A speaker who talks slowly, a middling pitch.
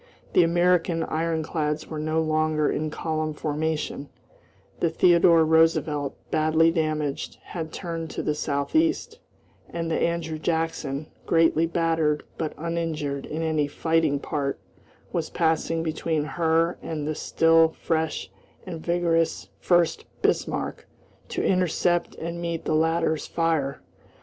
Yes: slow, 125 wpm; medium, 160 Hz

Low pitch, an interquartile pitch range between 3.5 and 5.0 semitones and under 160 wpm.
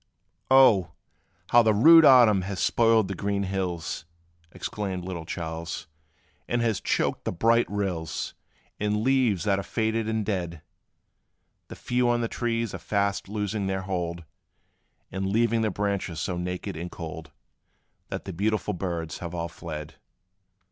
Yes: low, 100 Hz; average, 4.1 semitones; average, 150 wpm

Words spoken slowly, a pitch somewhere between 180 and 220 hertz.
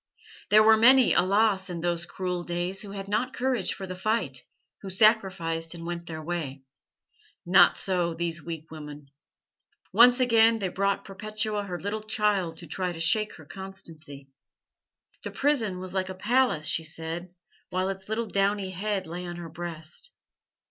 No: average, 165 wpm; medium, 185 Hz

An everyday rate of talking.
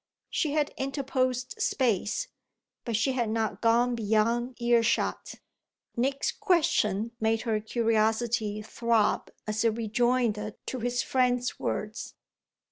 No: slow, 120 wpm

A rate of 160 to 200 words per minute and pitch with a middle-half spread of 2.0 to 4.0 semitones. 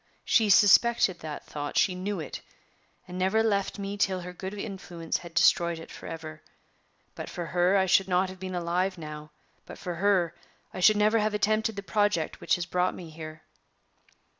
Yes: average, 185 wpm; average, 3.0 semitones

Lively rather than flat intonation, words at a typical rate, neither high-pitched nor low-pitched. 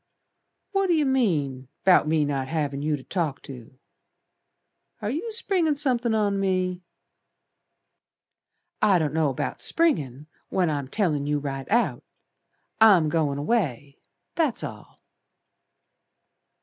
No: wide, 8.4 semitones; slow, 125 wpm; medium, 165 Hz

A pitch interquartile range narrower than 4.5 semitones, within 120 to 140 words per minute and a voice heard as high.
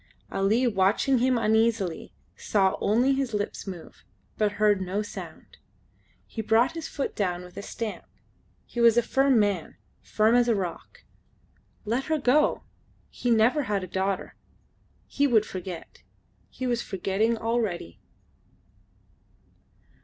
Yes: average, 3.9 semitones; slow, 135 wpm; high, 220 Hz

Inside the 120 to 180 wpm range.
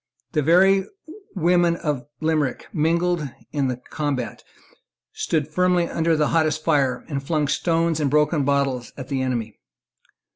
Yes: average, 140 wpm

